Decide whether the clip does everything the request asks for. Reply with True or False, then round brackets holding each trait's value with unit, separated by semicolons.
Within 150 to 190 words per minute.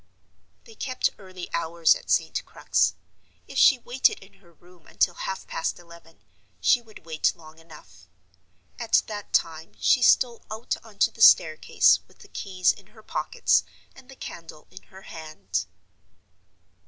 True (155 wpm)